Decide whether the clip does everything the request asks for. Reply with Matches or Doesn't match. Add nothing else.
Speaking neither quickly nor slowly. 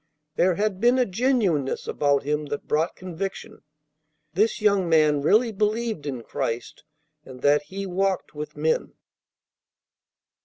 Doesn't match